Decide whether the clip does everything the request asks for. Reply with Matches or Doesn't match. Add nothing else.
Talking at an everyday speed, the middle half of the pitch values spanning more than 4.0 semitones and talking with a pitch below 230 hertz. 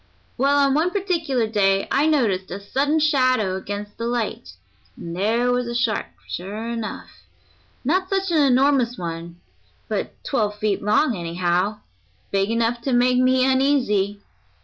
Doesn't match